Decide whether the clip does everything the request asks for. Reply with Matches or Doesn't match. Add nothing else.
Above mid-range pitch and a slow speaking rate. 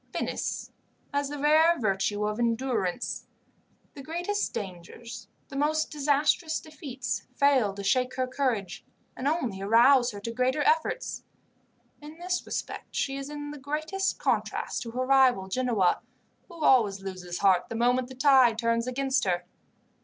Doesn't match